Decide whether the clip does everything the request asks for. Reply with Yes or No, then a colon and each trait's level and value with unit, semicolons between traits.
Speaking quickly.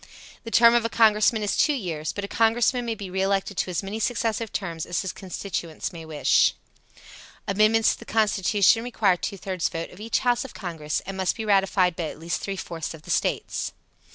Yes: fast, 210 wpm